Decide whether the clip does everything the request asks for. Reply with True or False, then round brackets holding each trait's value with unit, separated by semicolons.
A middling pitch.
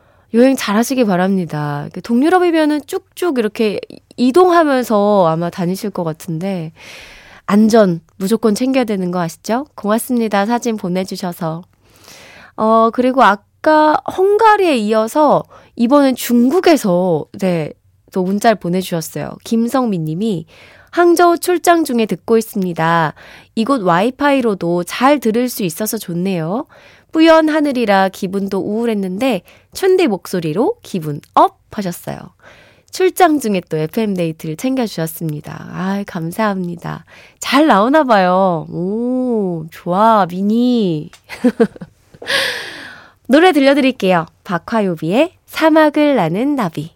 False (220 Hz)